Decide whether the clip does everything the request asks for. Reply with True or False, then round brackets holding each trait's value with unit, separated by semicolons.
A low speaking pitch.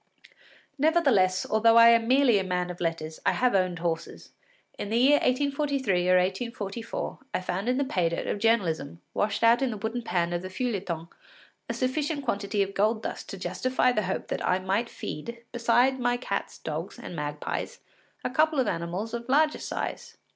False (220 Hz)